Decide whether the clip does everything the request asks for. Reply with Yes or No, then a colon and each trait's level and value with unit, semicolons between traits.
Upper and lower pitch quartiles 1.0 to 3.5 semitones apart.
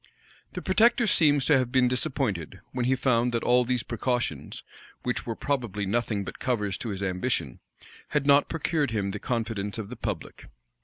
No: average, 4.0 semitones